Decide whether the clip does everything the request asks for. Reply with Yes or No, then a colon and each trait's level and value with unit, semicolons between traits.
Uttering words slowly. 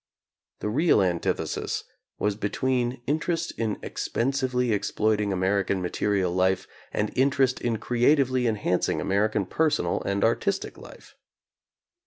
Yes: slow, 120 wpm